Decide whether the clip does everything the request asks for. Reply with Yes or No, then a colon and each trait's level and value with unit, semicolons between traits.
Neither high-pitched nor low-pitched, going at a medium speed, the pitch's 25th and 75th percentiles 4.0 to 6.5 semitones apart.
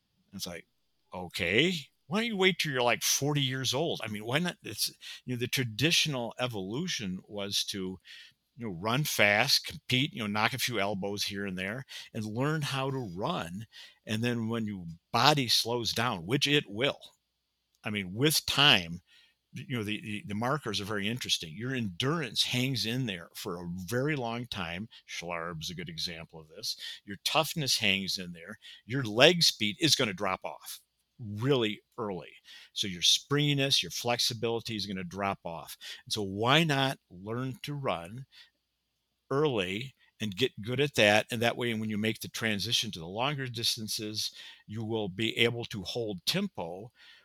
No: low, 115 Hz; average, 175 wpm; average, 4.8 semitones